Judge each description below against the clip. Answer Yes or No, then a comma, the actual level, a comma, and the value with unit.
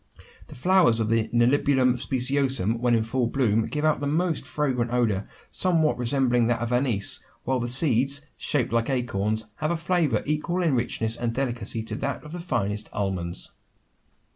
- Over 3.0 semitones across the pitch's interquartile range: Yes, average, 3.8 semitones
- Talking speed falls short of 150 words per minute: No, average, 170 wpm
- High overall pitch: No, low, 125 Hz